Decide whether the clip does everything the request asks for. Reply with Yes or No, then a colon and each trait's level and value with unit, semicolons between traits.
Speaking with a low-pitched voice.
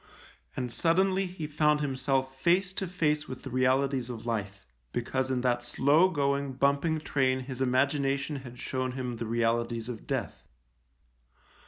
Yes: low, 130 Hz